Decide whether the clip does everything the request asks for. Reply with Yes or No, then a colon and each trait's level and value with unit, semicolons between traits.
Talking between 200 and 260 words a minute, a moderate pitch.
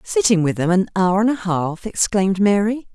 No: fast, 205 wpm; high, 195 Hz